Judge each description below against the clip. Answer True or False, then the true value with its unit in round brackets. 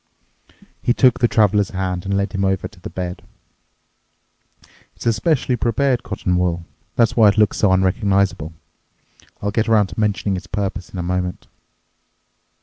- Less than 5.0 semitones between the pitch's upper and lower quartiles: True (2.8 semitones)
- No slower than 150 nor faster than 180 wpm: True (160 wpm)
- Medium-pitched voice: False (100 Hz)